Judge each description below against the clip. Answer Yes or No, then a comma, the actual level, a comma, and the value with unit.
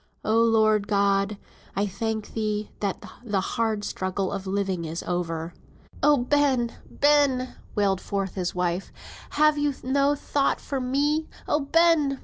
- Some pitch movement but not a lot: No, wide, 6.0 semitones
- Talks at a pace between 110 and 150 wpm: Yes, average, 140 wpm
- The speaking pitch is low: No, high, 220 Hz